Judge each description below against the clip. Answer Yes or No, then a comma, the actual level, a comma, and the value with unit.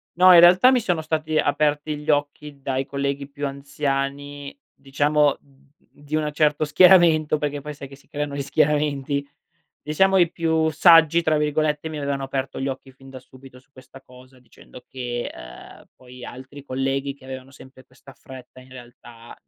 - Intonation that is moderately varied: No, narrow, 2.3 semitones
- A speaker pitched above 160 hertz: No, medium, 140 Hz